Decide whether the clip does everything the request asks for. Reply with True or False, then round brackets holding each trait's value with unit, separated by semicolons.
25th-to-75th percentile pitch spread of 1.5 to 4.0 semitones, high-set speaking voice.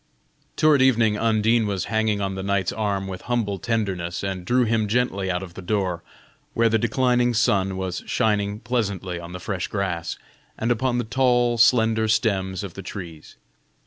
False (3.4 semitones; 105 Hz)